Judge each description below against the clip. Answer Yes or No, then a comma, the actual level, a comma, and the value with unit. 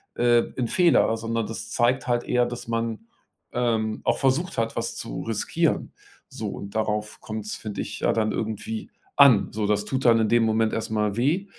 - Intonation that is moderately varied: No, narrow, 1.9 semitones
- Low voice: Yes, low, 115 Hz